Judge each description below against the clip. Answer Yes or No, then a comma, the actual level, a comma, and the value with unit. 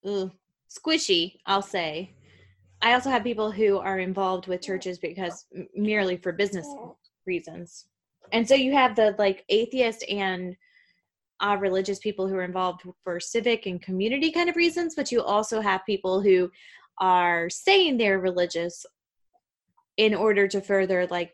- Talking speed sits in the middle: Yes, average, 155 wpm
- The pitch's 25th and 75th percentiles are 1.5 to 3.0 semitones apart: No, average, 4.0 semitones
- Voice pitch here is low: No, high, 195 Hz